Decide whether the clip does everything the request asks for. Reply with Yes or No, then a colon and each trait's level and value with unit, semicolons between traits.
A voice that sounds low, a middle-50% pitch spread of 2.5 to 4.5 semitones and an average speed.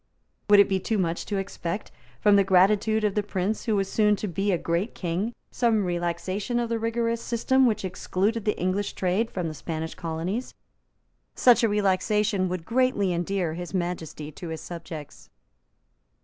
No: high, 195 Hz; average, 3.6 semitones; average, 175 wpm